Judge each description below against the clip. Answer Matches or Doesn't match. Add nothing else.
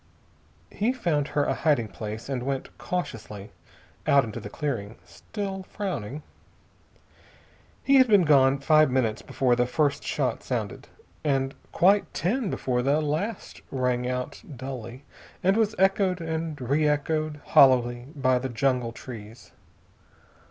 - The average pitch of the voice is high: Doesn't match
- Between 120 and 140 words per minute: Matches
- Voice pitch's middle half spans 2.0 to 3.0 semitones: Doesn't match